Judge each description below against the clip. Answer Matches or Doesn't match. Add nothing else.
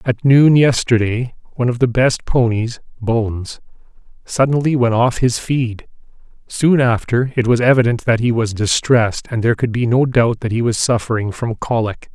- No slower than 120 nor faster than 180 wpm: Matches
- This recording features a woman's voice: Doesn't match